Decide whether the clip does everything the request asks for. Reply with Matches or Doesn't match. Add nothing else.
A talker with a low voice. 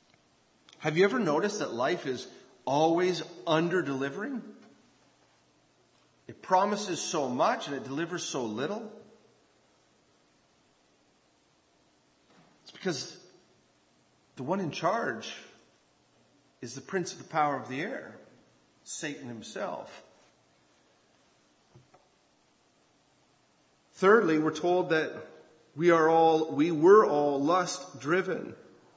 Doesn't match